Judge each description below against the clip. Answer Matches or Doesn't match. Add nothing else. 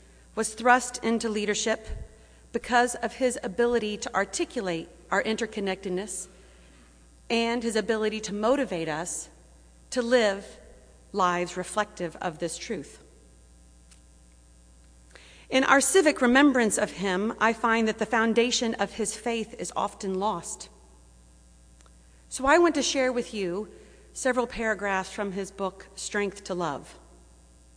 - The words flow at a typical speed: Doesn't match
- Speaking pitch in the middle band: Doesn't match